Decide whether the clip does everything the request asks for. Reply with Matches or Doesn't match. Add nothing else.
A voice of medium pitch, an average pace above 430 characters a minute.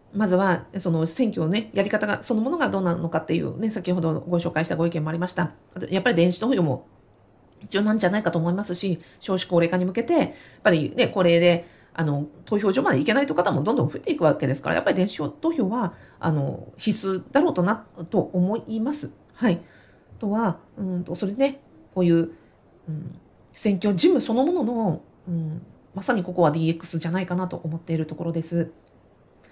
Doesn't match